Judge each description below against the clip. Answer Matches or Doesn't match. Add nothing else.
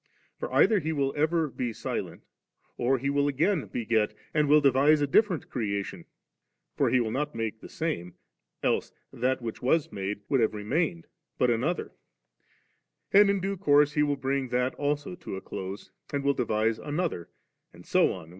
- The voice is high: Doesn't match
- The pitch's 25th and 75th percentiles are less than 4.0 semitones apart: Doesn't match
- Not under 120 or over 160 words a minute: Doesn't match